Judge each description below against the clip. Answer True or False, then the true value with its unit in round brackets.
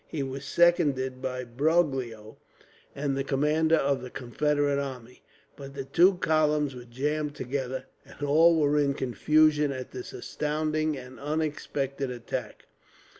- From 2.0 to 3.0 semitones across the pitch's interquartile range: True (2.7 semitones)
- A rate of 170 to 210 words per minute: False (135 wpm)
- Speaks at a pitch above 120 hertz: True (140 Hz)